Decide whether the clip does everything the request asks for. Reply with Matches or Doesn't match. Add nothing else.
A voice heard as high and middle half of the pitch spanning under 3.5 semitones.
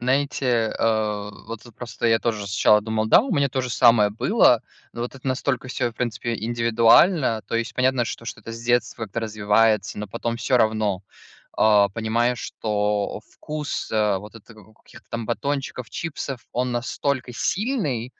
Doesn't match